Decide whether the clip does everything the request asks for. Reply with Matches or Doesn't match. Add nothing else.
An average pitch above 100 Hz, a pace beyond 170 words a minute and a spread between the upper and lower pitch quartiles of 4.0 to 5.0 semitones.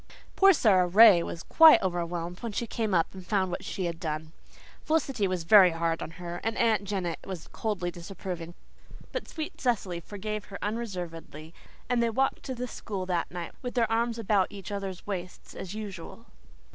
Matches